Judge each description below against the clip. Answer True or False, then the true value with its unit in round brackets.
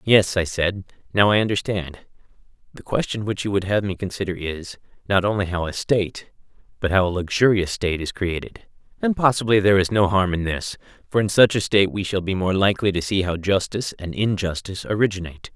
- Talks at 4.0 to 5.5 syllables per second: False (6.0 syllables/s)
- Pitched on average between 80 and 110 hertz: True (95 Hz)